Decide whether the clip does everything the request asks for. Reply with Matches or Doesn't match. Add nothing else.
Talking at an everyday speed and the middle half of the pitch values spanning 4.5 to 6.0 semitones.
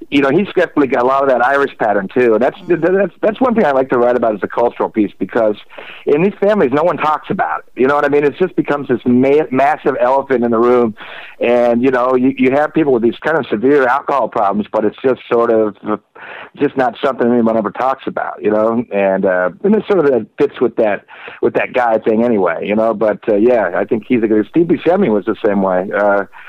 Doesn't match